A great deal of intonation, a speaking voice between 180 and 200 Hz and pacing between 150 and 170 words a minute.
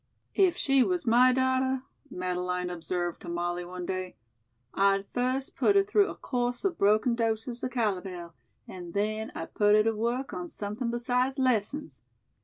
No: wide, 5.9 semitones; high, 220 Hz; average, 165 wpm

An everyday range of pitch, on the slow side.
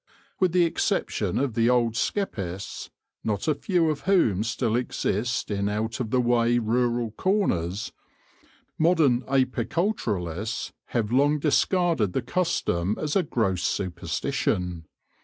No: wide, 6.6 semitones; slow, 125 wpm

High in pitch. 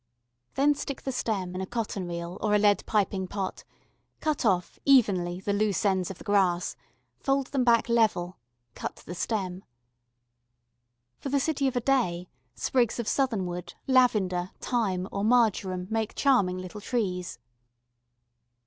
Yes: high, 205 Hz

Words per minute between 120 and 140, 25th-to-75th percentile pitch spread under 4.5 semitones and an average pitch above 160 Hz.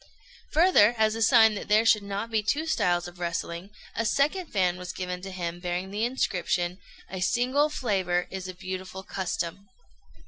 No: average, 175 wpm; average, 4.0 semitones; high, 190 Hz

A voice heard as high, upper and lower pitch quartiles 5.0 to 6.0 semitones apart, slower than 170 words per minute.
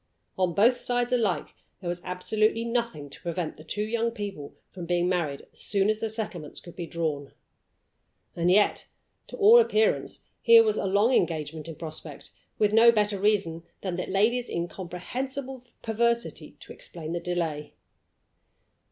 Yes: high, 195 Hz; wide, 5.5 semitones; average, 160 wpm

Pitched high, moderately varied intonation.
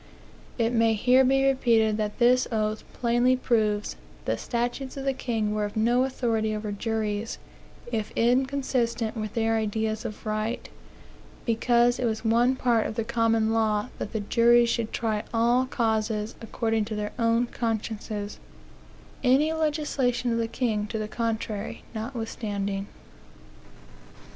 No: high, 230 Hz; narrow, 2.0 semitones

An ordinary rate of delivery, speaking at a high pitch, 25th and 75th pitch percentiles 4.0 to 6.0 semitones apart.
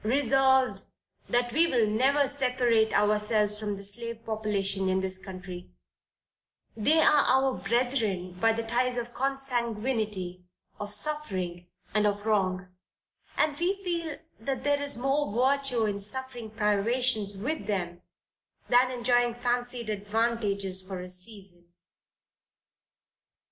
No: slow, 120 wpm; high, 225 Hz; average, 4.3 semitones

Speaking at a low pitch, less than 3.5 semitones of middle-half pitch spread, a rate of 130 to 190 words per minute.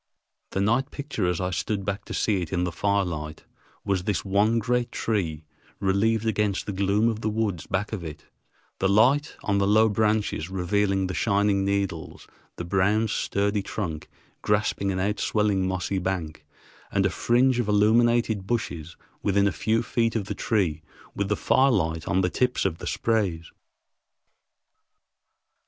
Yes: low, 100 Hz; average, 2.9 semitones; average, 160 wpm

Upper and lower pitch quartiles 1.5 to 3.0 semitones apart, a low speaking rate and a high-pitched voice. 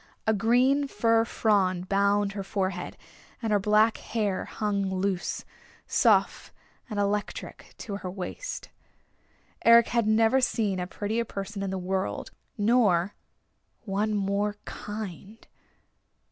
Yes: narrow, 2.4 semitones; slow, 120 wpm; high, 205 Hz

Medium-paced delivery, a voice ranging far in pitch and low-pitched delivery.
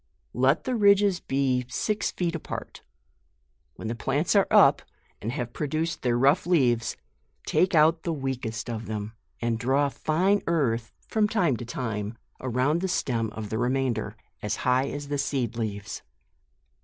Yes: average, 155 wpm; wide, 5.9 semitones; low, 130 Hz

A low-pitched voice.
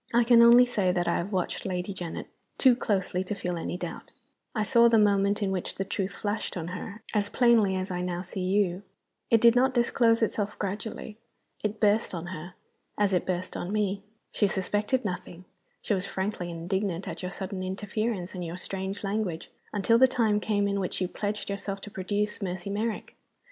No: high, 200 Hz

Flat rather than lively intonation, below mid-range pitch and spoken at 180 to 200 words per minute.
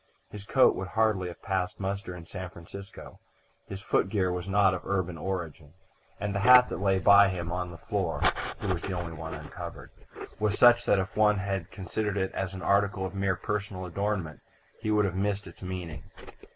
Yes: narrow, 1.9 semitones; very low, 95 Hz; average, 195 wpm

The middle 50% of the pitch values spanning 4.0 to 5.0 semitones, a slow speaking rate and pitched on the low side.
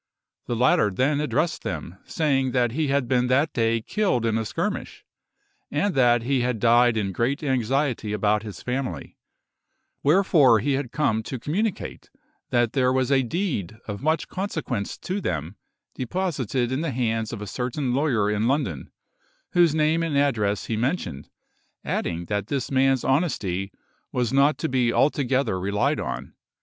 No: average, 4.4 semitones; average, 160 wpm; low, 125 Hz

